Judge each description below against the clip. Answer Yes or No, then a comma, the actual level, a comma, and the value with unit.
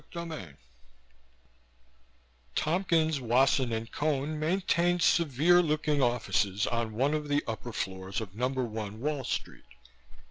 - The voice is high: No, low, 135 Hz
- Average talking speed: No, slow, 120 wpm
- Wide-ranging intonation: Yes, wide, 5.7 semitones